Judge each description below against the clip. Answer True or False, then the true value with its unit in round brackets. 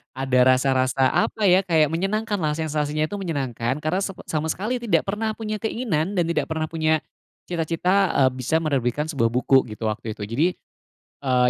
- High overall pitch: False (155 Hz)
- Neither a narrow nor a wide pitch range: False (6.0 semitones)